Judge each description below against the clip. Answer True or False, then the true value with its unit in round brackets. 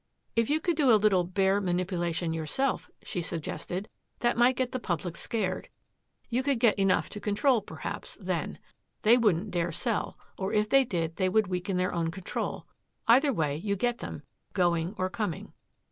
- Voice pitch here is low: False (195 Hz)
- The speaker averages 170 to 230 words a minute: True (175 wpm)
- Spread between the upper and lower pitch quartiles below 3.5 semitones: False (4.9 semitones)